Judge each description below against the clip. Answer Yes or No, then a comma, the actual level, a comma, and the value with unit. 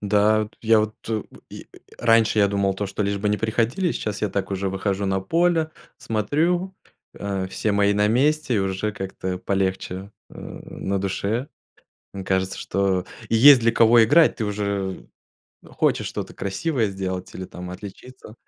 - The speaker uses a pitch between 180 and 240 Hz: No, low, 105 Hz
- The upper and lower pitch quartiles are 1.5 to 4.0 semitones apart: Yes, average, 2.9 semitones